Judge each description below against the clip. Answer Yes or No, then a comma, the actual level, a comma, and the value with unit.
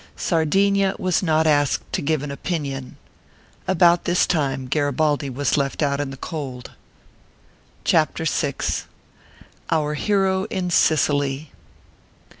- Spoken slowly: Yes, slow, 115 wpm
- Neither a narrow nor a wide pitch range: Yes, average, 3.9 semitones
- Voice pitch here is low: No, medium, 150 Hz